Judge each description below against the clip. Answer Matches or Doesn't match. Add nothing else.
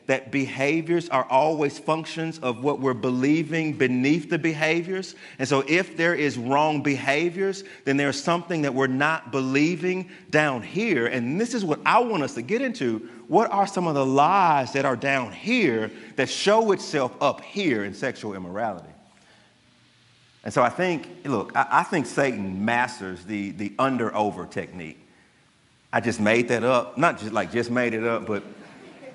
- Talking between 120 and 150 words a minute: Doesn't match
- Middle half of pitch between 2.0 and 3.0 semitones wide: Doesn't match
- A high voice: Doesn't match